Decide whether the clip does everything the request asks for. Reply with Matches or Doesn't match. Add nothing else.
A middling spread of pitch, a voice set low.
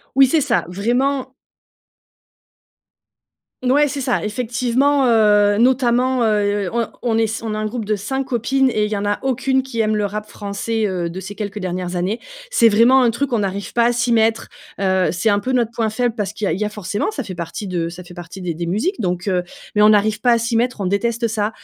Doesn't match